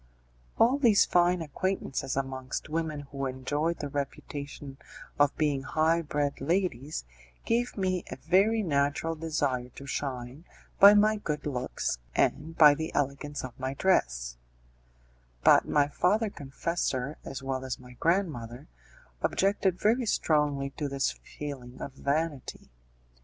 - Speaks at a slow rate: Yes, slow, 130 wpm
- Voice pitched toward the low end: No, medium, 145 Hz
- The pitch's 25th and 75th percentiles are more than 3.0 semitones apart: Yes, average, 4.1 semitones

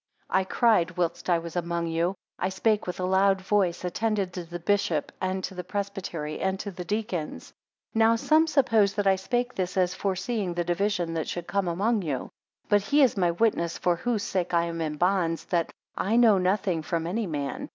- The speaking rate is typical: No, fast, 215 wpm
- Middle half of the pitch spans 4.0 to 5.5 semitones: No, average, 3.3 semitones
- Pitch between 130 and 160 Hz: No, medium, 185 Hz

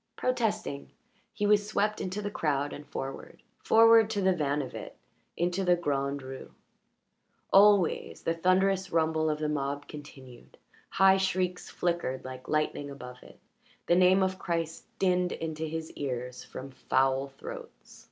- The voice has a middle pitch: Yes, medium, 165 Hz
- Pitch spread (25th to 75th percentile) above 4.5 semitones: Yes, average, 5.2 semitones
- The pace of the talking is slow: No, average, 150 wpm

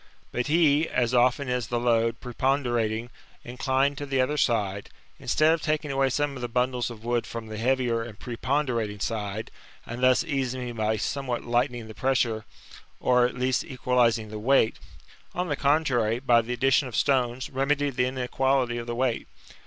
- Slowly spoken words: No, average, 175 wpm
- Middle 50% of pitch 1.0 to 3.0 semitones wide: Yes, narrow, 2.4 semitones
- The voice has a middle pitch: No, low, 125 Hz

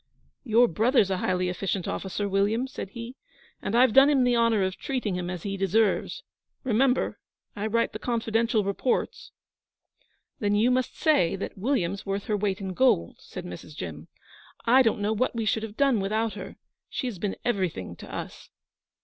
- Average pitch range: Yes, average, 3.9 semitones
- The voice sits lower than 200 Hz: No, high, 215 Hz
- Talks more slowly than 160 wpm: No, average, 180 wpm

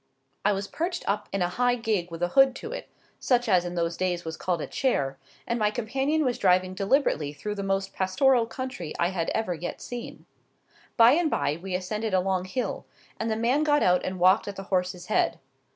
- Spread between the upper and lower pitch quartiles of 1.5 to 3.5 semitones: No, average, 5.2 semitones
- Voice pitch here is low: No, high, 195 Hz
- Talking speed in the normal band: No, fast, 215 wpm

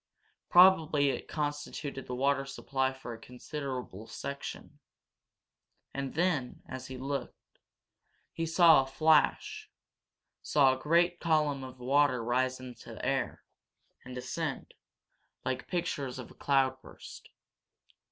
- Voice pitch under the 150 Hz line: Yes, low, 135 Hz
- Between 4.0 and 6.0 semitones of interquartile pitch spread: No, narrow, 2.6 semitones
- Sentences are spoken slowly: Yes, slow, 120 wpm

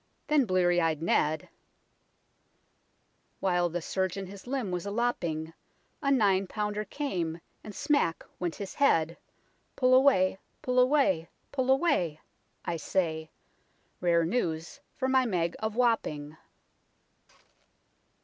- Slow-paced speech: Yes, slow, 120 wpm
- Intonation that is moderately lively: No, wide, 7.0 semitones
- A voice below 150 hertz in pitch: No, high, 190 Hz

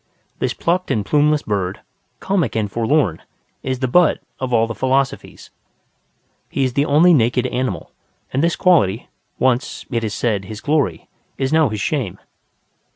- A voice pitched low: Yes, low, 130 Hz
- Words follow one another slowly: No, average, 160 wpm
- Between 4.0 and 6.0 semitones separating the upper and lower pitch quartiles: Yes, average, 5.2 semitones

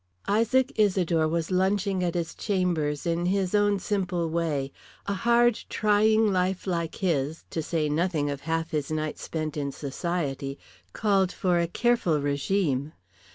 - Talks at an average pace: Yes, average, 150 wpm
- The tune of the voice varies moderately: Yes, average, 4.2 semitones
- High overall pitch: No, medium, 175 Hz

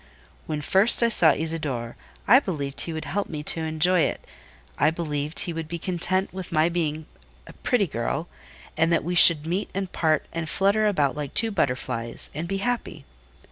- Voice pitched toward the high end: No, medium, 165 Hz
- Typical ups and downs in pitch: Yes, average, 3.7 semitones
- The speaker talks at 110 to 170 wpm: No, average, 185 wpm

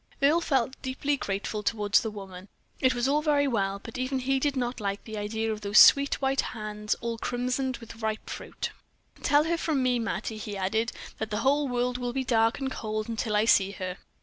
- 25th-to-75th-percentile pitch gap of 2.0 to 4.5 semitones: Yes, average, 3.9 semitones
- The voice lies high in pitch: Yes, high, 230 Hz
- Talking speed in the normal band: No, fast, 210 wpm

